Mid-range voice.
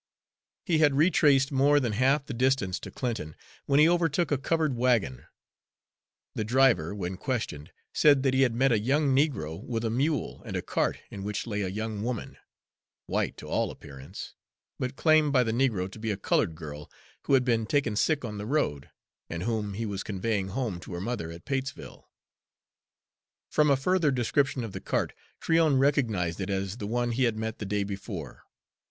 No: low, 120 Hz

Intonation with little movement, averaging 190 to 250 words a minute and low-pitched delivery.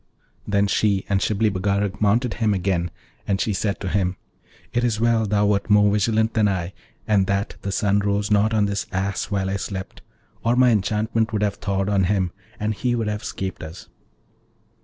Yes: narrow, 1.8 semitones; average, 195 wpm; low, 100 Hz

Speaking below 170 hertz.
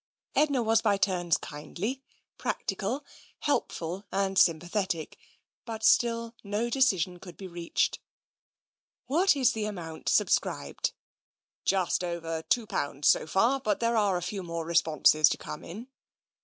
No: high, 195 Hz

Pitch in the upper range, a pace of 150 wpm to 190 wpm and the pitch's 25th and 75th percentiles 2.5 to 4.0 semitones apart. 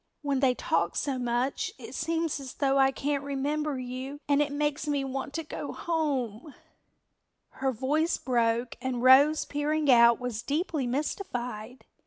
Yes: very high, 270 Hz; average, 155 wpm; average, 2.8 semitones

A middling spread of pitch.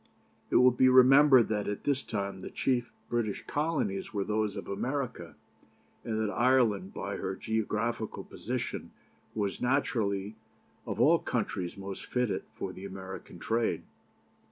Yes: average, 4.1 semitones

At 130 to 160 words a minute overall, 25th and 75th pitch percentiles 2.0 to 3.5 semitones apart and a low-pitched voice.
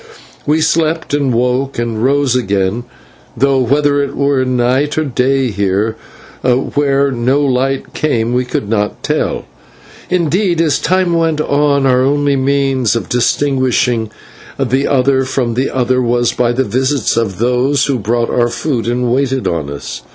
Yes: average, 155 wpm; average, 2.8 semitones; low, 130 Hz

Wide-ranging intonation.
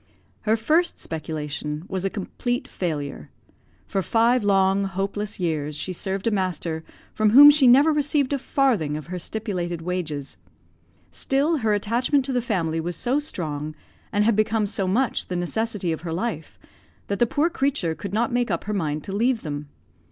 Yes: wide, 6.4 semitones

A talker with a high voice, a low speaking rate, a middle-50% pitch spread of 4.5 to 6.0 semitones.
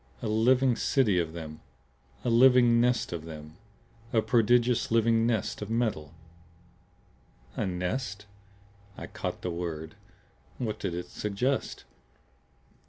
No: low, 110 Hz; slow, 120 wpm; wide, 5.6 semitones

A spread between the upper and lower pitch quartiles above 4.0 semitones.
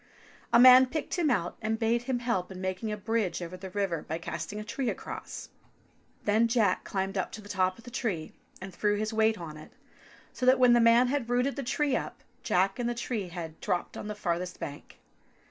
Yes: average, 4.6 semitones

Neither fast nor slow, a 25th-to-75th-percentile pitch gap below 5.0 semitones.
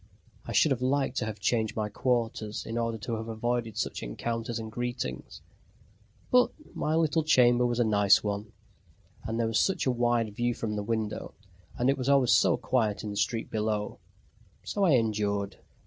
Yes: average, 185 wpm; narrow, 2.4 semitones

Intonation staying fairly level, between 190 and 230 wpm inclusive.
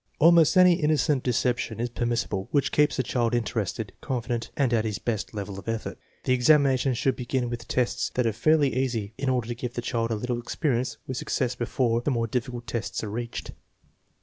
Yes: narrow, 2.2 semitones; average, 200 wpm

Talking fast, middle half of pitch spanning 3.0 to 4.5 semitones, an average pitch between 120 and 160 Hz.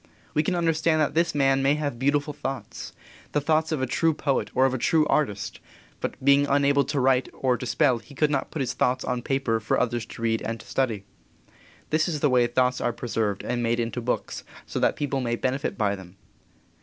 Yes: fast, 220 wpm; average, 3.5 semitones; low, 135 Hz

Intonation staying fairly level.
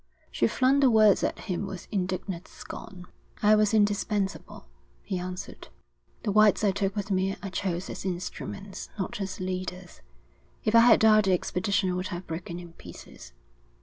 Yes: narrow, 2.3 semitones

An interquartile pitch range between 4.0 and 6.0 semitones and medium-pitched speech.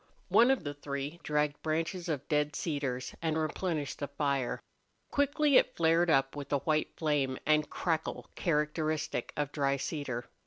No: narrow, 2.5 semitones; medium, 150 Hz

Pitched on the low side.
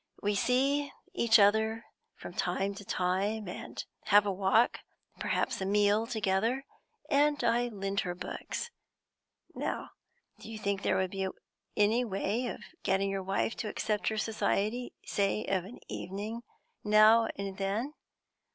No: high, 210 Hz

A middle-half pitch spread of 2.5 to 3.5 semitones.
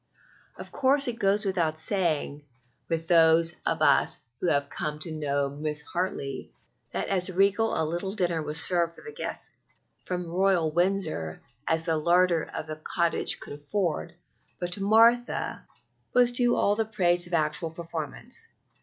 No: average, 3.9 semitones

